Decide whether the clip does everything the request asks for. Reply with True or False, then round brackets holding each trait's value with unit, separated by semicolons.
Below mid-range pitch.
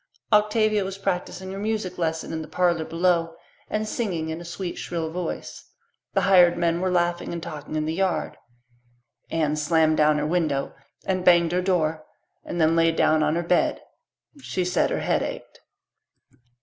False (175 Hz)